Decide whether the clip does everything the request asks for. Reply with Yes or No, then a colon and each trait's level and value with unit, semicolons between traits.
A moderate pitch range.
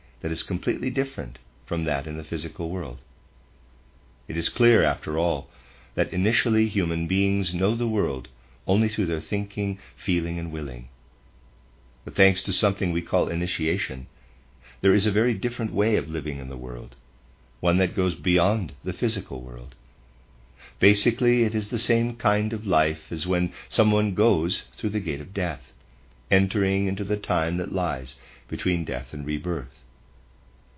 No: wide, 7.9 semitones